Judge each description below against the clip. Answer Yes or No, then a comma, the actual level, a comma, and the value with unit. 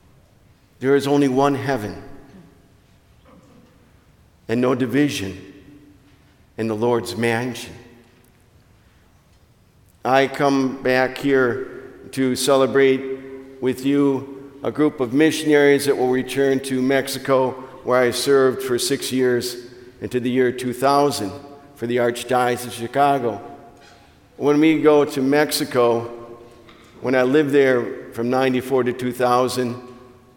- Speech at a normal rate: No, slow, 115 wpm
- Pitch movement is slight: Yes, narrow, 2.3 semitones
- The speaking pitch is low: Yes, low, 130 Hz